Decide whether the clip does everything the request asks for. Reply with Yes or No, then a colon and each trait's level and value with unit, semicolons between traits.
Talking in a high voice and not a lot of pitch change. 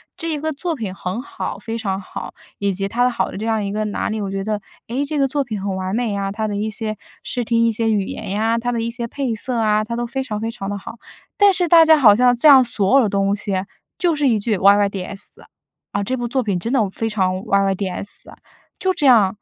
No: high, 220 Hz; average, 3.6 semitones